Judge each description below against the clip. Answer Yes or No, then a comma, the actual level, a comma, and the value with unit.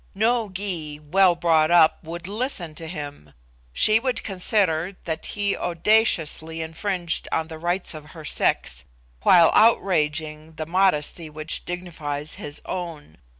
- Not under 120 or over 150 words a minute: Yes, slow, 135 wpm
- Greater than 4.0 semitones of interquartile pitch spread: No, average, 3.4 semitones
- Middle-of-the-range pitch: Yes, medium, 165 Hz